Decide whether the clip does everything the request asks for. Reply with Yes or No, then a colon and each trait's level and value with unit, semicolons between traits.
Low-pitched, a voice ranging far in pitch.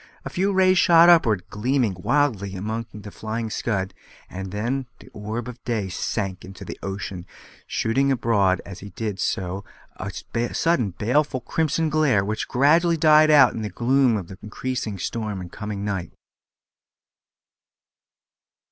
Yes: low, 110 Hz; wide, 5.7 semitones